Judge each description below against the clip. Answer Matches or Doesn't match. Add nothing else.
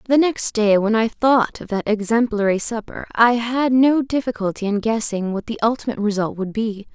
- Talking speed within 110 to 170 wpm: Doesn't match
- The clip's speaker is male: Doesn't match